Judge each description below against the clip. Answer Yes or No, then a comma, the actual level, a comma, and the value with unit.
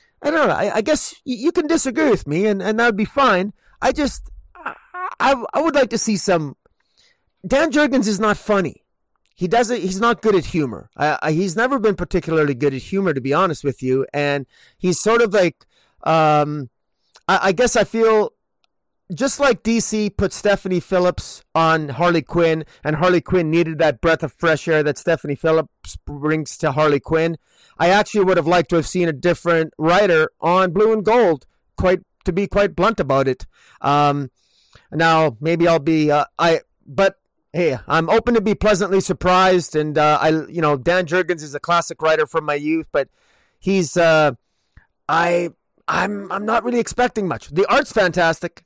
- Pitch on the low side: No, medium, 175 Hz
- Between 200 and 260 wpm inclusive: No, average, 185 wpm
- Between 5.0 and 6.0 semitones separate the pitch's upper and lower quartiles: Yes, average, 5.3 semitones